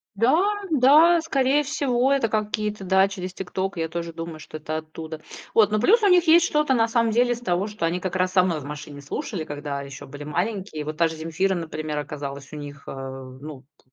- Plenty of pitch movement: Yes, wide, 7.0 semitones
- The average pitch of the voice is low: No, medium, 185 Hz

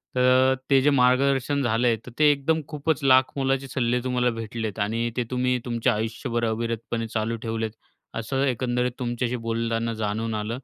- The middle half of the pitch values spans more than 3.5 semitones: No, narrow, 2.4 semitones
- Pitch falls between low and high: No, low, 120 Hz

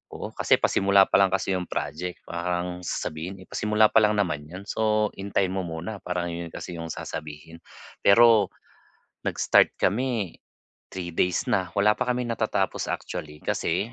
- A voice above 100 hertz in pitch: No, very low, 95 Hz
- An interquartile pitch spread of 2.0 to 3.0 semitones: No, average, 3.7 semitones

